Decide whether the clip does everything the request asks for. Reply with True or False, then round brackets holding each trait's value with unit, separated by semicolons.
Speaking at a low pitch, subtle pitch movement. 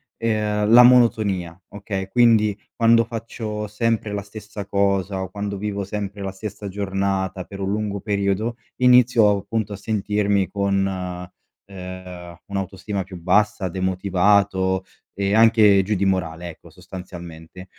True (100 Hz; 1.9 semitones)